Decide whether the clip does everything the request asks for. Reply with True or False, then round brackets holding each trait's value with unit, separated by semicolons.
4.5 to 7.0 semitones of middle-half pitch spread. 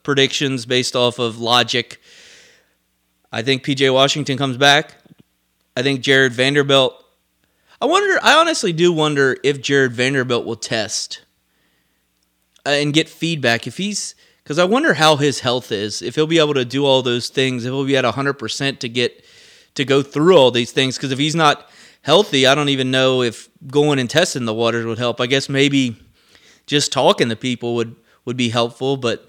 False (3.3 semitones)